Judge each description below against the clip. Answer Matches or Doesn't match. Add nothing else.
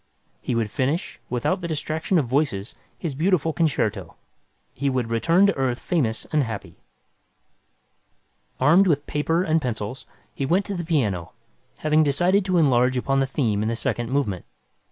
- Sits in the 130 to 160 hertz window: Matches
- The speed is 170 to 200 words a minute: Doesn't match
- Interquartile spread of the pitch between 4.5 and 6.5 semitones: Matches